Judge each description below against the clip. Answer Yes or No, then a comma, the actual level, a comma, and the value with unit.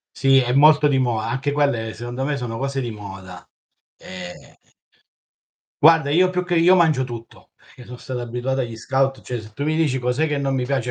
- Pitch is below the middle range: Yes, low, 130 Hz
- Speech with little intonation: No, average, 3.3 semitones